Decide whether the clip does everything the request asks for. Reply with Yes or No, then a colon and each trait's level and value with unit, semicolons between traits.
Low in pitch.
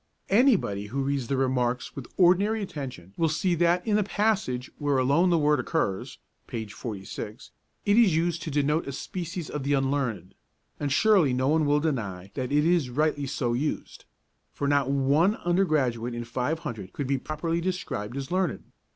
No: medium, 145 Hz